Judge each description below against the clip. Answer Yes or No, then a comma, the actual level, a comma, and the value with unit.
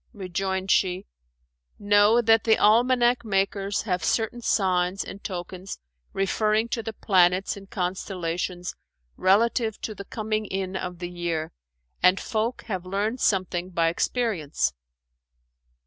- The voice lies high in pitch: Yes, high, 195 Hz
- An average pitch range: Yes, average, 3.2 semitones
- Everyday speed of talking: No, slow, 125 wpm